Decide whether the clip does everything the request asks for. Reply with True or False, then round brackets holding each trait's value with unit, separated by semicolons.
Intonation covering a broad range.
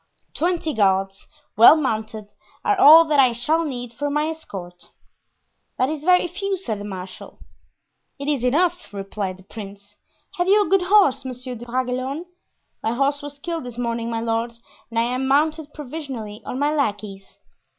True (5.9 semitones)